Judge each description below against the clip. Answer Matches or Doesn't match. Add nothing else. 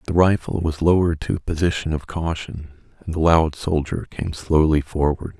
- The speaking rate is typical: Matches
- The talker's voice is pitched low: Matches